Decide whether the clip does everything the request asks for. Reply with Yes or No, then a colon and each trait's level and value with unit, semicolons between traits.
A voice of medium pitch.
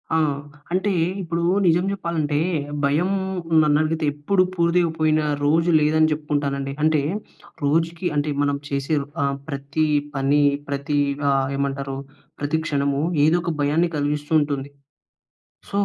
Yes: medium, 150 Hz